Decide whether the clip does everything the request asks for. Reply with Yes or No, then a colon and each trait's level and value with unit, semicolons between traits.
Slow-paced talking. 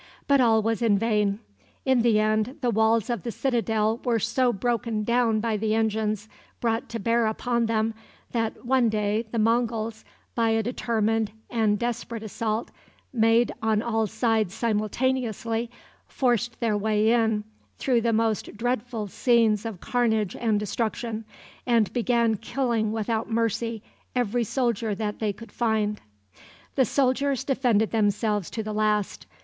No: average, 145 wpm